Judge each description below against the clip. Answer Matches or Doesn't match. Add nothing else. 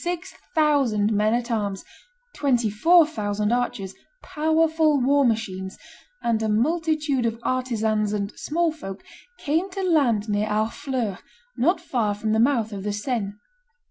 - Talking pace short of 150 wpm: Matches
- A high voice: Matches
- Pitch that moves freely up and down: Matches